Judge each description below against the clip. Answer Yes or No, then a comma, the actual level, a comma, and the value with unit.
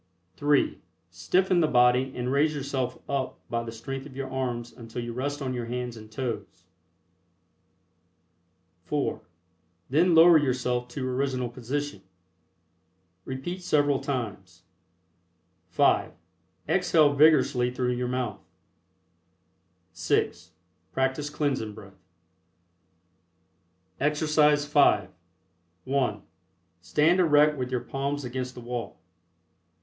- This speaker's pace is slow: Yes, slow, 105 wpm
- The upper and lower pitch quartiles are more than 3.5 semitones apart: No, average, 3.0 semitones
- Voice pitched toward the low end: Yes, low, 130 Hz